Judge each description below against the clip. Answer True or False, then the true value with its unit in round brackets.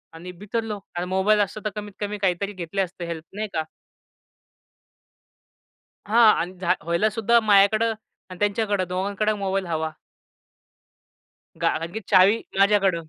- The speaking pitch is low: False (200 Hz)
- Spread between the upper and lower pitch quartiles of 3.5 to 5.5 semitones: False (2.7 semitones)